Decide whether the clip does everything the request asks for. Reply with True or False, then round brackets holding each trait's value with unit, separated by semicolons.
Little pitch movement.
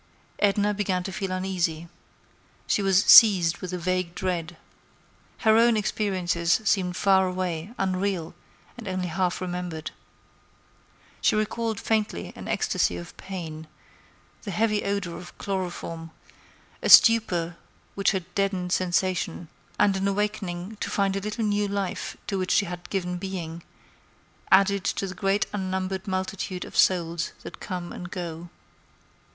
True (2.2 semitones)